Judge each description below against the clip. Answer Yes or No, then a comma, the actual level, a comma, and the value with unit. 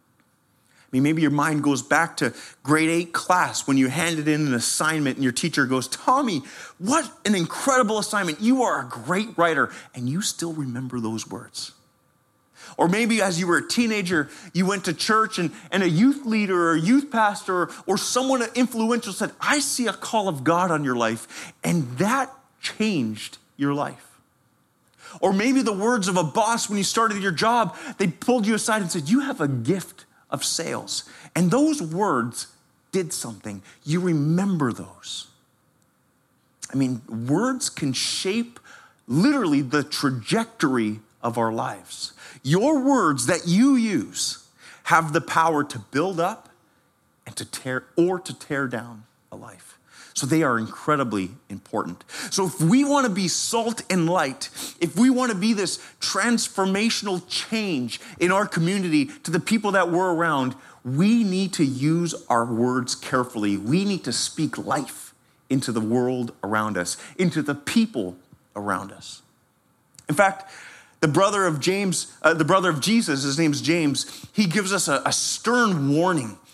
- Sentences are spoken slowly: No, average, 165 wpm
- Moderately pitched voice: Yes, medium, 175 Hz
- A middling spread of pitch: No, wide, 7.2 semitones